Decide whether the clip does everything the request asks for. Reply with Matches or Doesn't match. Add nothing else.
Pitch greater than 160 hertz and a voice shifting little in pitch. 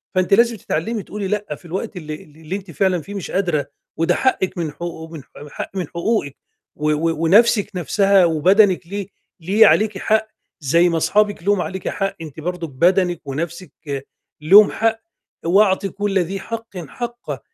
Doesn't match